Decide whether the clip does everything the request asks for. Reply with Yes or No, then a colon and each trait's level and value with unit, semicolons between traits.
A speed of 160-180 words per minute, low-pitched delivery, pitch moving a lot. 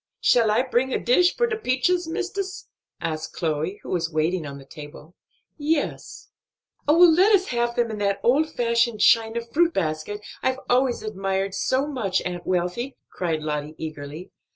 No: average, 165 wpm; high, 225 Hz; wide, 7.9 semitones